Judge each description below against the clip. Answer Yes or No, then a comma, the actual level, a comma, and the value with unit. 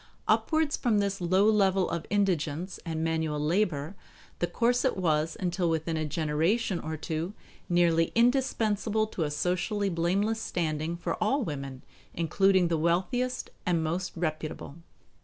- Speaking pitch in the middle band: Yes, medium, 175 Hz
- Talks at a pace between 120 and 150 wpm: Yes, average, 140 wpm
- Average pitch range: Yes, average, 4.3 semitones